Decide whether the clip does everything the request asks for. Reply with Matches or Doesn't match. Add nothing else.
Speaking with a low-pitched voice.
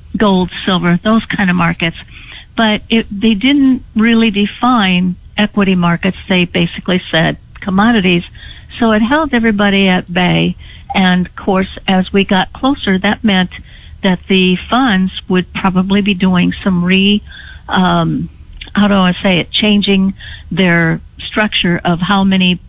Doesn't match